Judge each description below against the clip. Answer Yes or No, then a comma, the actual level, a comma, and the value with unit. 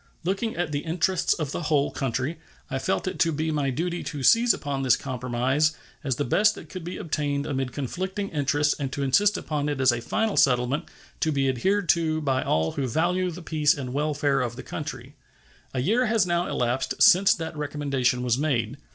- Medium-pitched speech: Yes, medium, 145 Hz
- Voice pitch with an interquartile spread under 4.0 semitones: No, average, 4.5 semitones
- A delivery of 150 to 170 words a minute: No, fast, 205 wpm